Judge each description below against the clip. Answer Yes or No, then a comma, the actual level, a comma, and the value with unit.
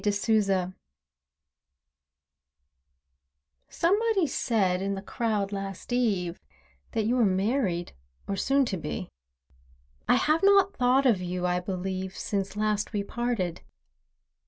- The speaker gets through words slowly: Yes, slow, 120 wpm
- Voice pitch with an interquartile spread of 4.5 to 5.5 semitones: Yes, average, 4.8 semitones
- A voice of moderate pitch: No, high, 205 Hz